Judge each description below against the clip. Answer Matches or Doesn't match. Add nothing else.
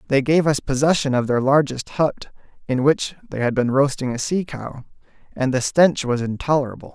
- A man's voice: Matches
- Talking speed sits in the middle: Matches